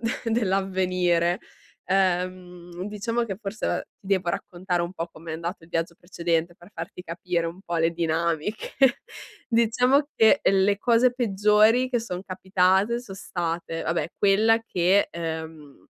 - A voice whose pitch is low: No, medium, 185 Hz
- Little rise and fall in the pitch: No, average, 3.6 semitones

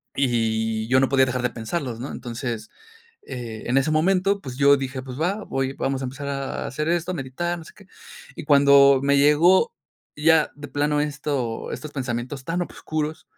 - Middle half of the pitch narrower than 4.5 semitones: Yes, average, 3.3 semitones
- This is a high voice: No, medium, 140 Hz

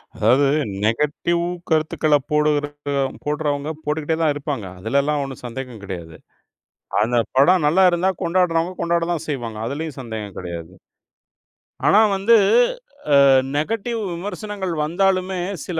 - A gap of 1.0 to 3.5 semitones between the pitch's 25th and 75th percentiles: No, average, 4.8 semitones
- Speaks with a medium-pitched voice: Yes, medium, 150 Hz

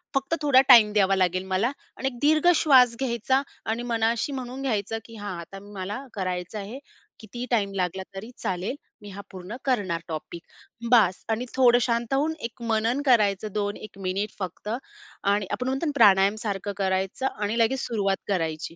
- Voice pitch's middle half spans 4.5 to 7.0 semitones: No, average, 4.1 semitones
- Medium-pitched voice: No, high, 215 Hz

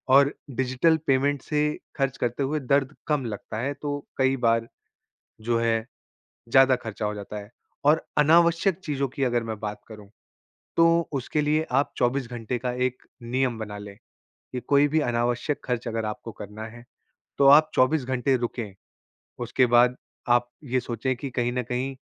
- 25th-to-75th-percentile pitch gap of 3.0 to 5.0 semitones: Yes, average, 3.3 semitones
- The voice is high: No, low, 125 Hz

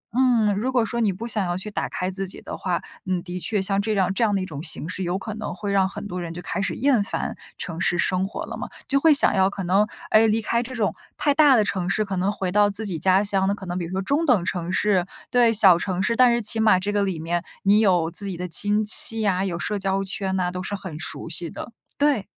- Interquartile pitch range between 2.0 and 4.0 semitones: Yes, average, 2.9 semitones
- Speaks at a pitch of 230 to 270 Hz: No, high, 195 Hz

